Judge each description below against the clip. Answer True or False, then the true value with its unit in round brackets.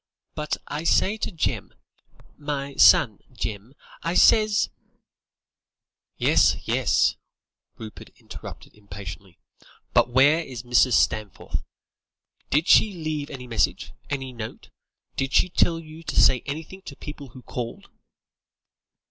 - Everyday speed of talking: False (120 wpm)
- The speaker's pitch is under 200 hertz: True (140 Hz)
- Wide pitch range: False (4.9 semitones)